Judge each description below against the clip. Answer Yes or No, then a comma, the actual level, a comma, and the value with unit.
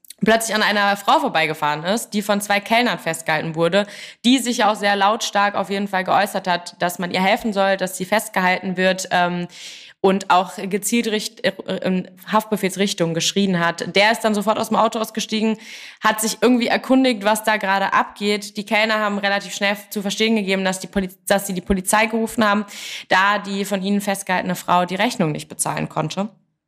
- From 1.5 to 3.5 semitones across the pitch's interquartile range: Yes, narrow, 2.6 semitones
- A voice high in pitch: Yes, high, 200 Hz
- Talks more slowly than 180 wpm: No, fast, 190 wpm